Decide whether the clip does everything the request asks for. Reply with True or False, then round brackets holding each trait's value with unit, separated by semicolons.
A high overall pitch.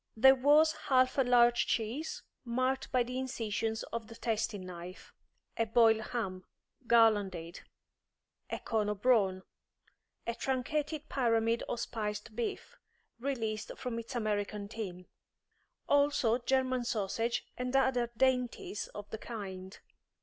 True (230 Hz)